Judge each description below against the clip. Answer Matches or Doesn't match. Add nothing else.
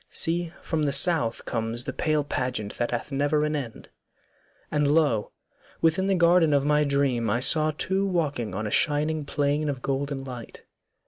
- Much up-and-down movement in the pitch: Doesn't match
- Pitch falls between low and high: Matches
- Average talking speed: Matches